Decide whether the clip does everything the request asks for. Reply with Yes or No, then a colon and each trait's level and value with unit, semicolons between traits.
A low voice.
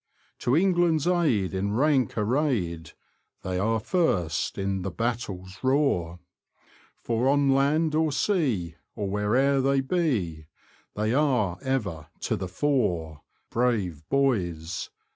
Yes: low, 115 Hz